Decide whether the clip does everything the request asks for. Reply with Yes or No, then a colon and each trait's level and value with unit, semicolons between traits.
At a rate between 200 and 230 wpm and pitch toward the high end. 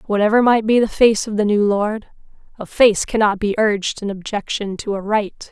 Yes: fast, 205 wpm; high, 210 Hz